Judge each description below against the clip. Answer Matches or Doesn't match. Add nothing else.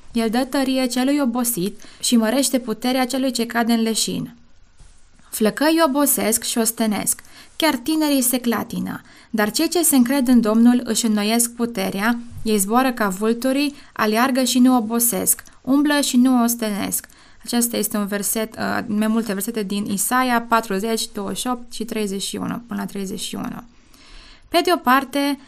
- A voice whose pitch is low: Doesn't match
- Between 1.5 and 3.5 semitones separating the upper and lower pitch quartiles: Matches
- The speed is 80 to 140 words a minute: Doesn't match